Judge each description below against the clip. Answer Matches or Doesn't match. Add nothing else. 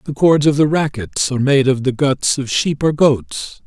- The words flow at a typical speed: Doesn't match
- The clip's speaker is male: Matches